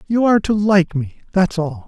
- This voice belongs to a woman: No, male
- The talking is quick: No, average, 190 wpm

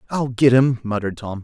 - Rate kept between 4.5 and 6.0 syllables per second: Yes, 5.8 syllables/s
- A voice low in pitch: Yes, low, 120 Hz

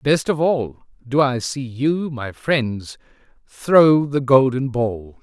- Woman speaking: No, male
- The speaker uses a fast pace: No, average, 150 wpm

